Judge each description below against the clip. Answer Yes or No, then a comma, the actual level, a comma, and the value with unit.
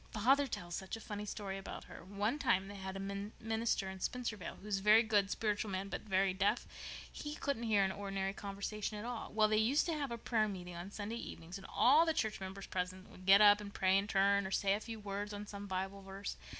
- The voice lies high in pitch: Yes, high, 205 Hz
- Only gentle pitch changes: Yes, narrow, 2.1 semitones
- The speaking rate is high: Yes, fast, 240 wpm